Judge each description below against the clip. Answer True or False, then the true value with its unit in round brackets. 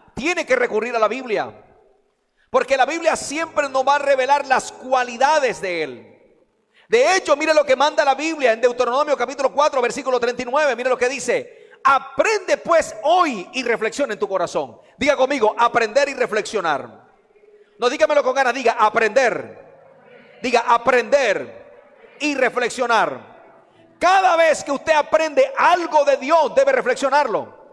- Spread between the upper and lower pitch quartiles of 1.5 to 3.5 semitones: False (4.1 semitones)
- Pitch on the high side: True (275 Hz)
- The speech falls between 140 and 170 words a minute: True (150 wpm)